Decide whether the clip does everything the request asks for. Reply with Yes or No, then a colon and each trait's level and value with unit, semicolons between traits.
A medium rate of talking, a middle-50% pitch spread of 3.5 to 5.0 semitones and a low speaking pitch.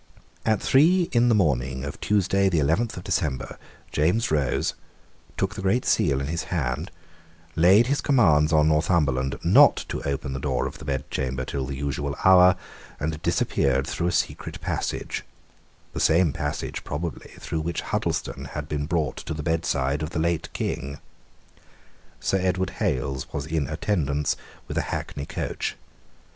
Yes: average, 160 wpm; average, 4.7 semitones; very low, 75 Hz